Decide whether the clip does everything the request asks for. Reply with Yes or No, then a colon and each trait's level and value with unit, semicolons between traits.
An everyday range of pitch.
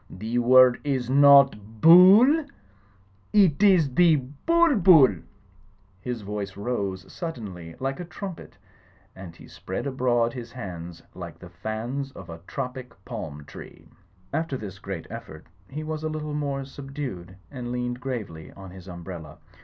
No: wide, 7.1 semitones